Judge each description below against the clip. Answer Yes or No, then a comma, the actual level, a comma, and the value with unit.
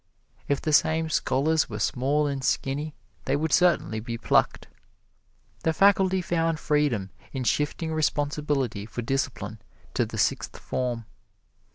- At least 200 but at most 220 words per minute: No, slow, 135 wpm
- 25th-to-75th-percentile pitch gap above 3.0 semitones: Yes, average, 3.7 semitones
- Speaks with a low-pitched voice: No, medium, 145 Hz